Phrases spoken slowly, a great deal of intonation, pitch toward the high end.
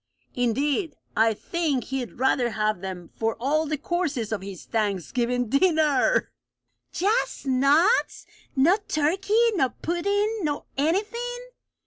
Yes: slow, 115 wpm; wide, 7.3 semitones; very high, 285 Hz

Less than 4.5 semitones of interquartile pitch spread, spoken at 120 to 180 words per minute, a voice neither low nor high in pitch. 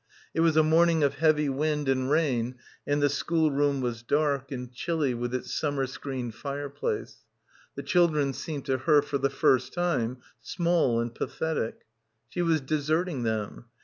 Yes: average, 3.3 semitones; average, 160 wpm; medium, 145 Hz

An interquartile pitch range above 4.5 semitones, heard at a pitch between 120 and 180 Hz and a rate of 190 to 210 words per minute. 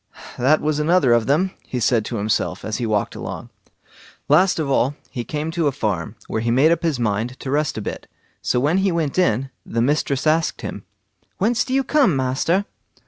Yes: wide, 5.6 semitones; medium, 140 Hz; fast, 205 wpm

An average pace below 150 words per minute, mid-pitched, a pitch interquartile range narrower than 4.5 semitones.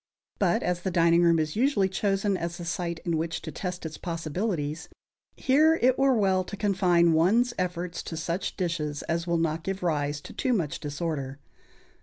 No: average, 185 wpm; medium, 175 Hz; average, 3.0 semitones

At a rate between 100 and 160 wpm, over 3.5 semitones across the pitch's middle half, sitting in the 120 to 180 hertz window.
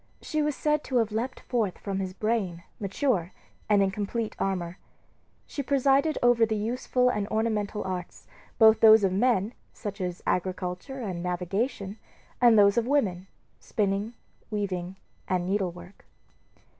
No: average, 145 wpm; average, 4.0 semitones; high, 210 Hz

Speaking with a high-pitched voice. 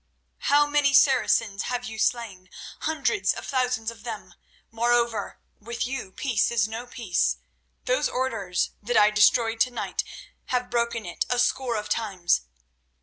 Yes: high, 235 Hz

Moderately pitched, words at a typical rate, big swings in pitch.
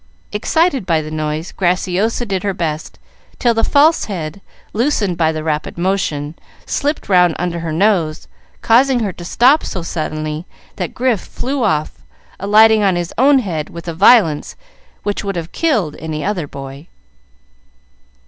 Yes: medium, 180 Hz; average, 155 wpm; wide, 5.9 semitones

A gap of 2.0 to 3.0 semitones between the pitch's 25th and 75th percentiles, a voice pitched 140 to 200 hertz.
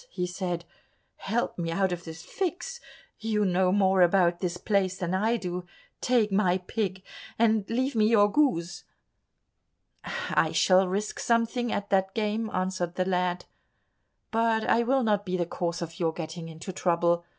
No: average, 3.7 semitones; high, 190 Hz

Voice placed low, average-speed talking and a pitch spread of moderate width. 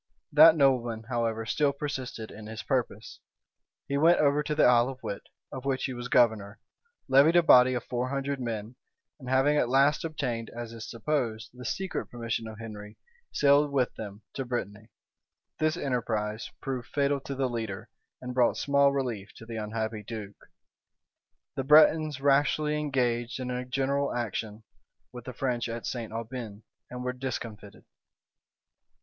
Yes: low, 125 Hz; average, 160 wpm; average, 3.5 semitones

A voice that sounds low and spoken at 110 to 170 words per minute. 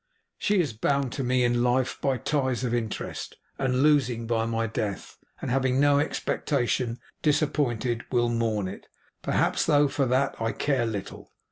Yes: low, 125 Hz; average, 160 wpm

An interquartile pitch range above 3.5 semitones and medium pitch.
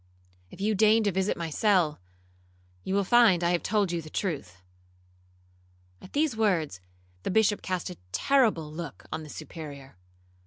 Yes: average, 5.1 semitones; medium, 180 Hz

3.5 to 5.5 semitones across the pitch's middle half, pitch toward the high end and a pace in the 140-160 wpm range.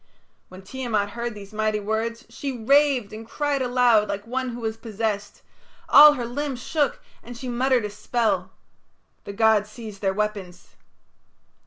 No: average, 3.1 semitones; high, 225 Hz; average, 155 wpm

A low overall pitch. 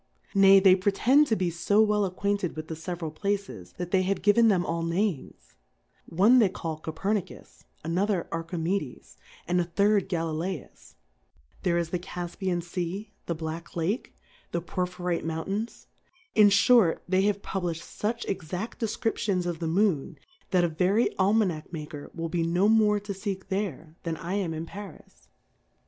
No: medium, 180 Hz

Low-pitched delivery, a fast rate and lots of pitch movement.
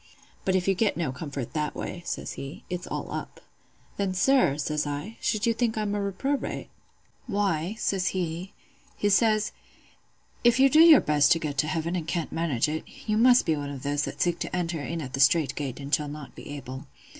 No: medium, 170 Hz; fast, 210 wpm; wide, 5.9 semitones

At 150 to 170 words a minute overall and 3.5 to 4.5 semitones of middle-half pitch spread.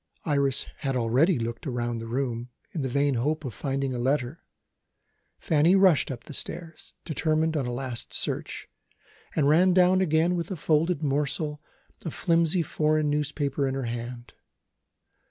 Yes: average, 155 wpm; average, 4.0 semitones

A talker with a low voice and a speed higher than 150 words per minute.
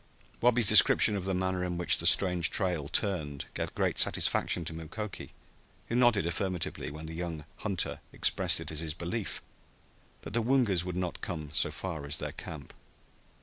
Yes: very low, 90 Hz; average, 175 wpm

